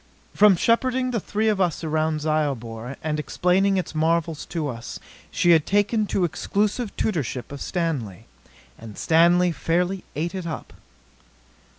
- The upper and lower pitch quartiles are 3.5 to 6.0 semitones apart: Yes, average, 4.2 semitones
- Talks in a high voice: No, medium, 170 Hz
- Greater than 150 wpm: No, average, 145 wpm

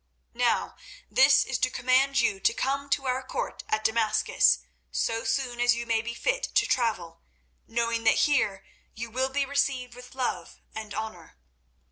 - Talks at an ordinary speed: Yes, average, 165 wpm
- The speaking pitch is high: Yes, high, 240 Hz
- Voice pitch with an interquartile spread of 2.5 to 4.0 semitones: Yes, average, 3.0 semitones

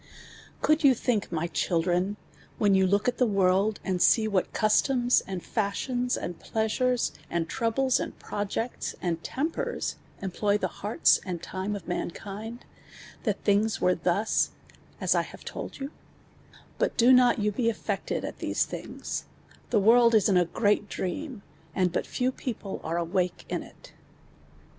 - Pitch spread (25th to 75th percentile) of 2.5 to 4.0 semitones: No, average, 4.6 semitones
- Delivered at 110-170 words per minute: Yes, average, 155 wpm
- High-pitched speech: Yes, high, 210 Hz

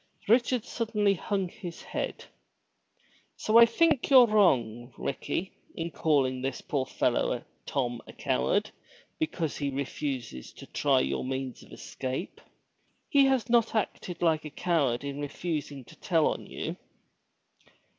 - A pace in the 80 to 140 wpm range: Yes, slow, 135 wpm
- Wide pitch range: Yes, wide, 8.1 semitones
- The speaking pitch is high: No, medium, 155 Hz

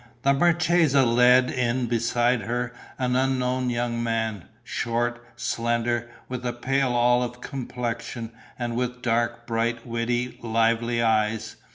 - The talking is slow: Yes, slow, 125 wpm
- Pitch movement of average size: No, narrow, 1.2 semitones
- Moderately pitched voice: No, low, 120 Hz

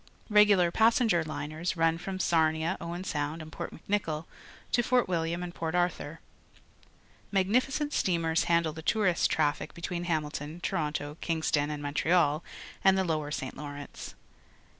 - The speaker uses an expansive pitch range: No, average, 3.1 semitones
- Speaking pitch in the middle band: Yes, medium, 165 Hz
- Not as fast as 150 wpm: Yes, average, 140 wpm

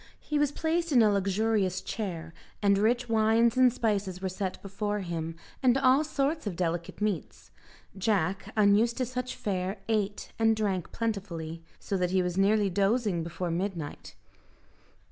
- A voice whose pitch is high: Yes, high, 205 Hz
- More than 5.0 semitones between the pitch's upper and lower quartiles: No, average, 3.7 semitones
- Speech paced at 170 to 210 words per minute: No, average, 155 wpm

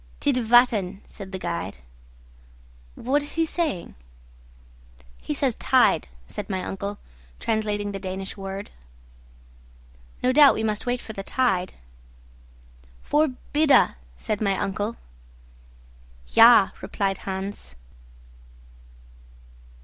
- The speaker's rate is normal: No, slow, 100 wpm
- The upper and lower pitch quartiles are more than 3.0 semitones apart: Yes, average, 4.6 semitones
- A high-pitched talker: Yes, high, 205 Hz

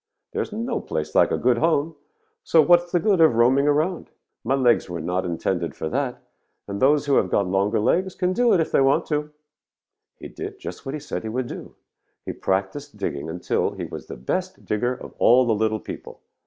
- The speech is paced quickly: Yes, fast, 220 wpm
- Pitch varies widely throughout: Yes, wide, 8.2 semitones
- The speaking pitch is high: No, low, 130 Hz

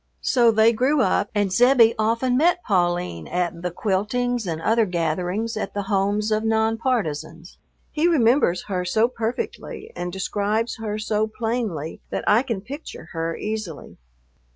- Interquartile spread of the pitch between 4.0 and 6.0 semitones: Yes, average, 4.3 semitones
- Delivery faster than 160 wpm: No, average, 155 wpm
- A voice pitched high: Yes, high, 215 Hz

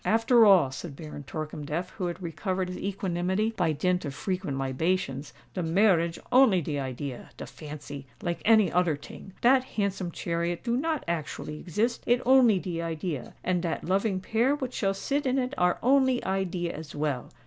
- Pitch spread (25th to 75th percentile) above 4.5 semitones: Yes, wide, 5.6 semitones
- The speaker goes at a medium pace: Yes, average, 170 wpm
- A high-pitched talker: No, medium, 180 Hz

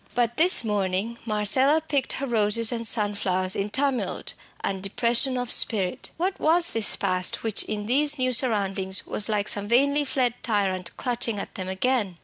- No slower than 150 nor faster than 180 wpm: Yes, average, 165 wpm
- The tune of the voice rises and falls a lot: No, average, 4.4 semitones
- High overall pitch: Yes, high, 225 Hz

